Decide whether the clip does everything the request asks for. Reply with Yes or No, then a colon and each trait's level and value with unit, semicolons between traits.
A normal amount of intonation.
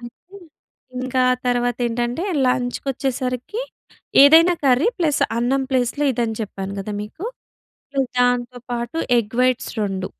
No: narrow, 2.2 semitones